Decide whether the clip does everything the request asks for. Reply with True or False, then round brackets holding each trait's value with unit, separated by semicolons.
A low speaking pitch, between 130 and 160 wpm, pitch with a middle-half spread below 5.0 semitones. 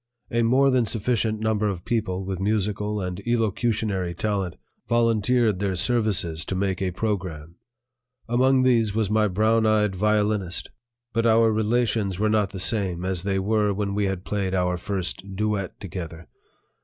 True (105 Hz; 155 wpm; 2.7 semitones)